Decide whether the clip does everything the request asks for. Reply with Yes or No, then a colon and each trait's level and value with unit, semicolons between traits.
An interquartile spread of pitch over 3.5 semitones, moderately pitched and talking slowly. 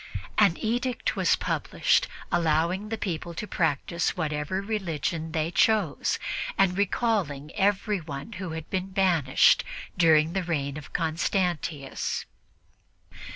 Yes: average, 3.9 semitones; medium, 175 Hz; slow, 110 wpm